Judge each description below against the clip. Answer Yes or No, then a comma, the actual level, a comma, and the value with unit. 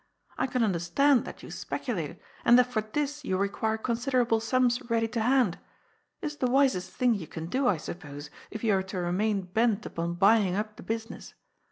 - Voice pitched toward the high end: Yes, high, 220 Hz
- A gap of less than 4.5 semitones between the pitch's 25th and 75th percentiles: No, average, 4.8 semitones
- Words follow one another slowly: No, fast, 205 wpm